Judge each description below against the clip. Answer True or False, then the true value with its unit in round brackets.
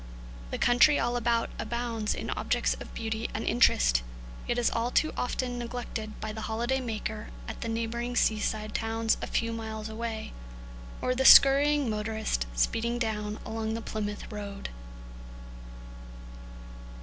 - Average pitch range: False (1.8 semitones)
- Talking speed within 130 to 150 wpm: True (140 wpm)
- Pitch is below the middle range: False (225 Hz)